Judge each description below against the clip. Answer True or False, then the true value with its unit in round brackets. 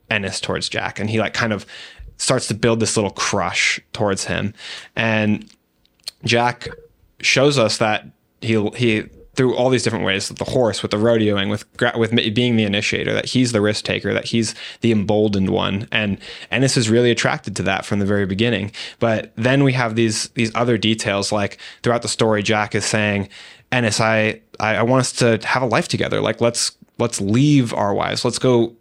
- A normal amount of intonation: False (2.3 semitones)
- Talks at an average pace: True (195 wpm)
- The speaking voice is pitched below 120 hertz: True (110 Hz)